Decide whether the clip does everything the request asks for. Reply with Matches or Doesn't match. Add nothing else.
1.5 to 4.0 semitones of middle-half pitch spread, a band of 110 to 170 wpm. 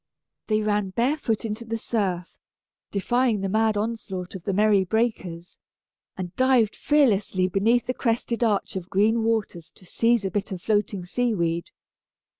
Matches